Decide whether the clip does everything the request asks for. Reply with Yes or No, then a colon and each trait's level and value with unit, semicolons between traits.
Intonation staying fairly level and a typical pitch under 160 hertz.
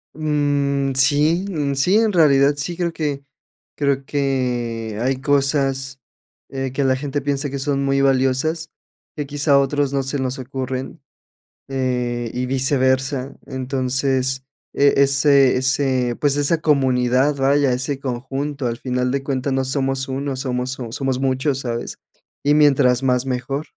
Yes: narrow, 1.6 semitones; low, 135 Hz